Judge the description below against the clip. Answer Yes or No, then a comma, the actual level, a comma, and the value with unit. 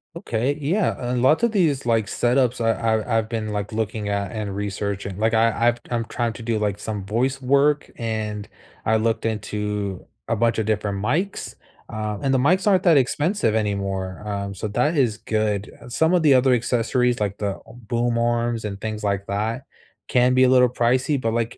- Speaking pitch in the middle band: No, low, 115 Hz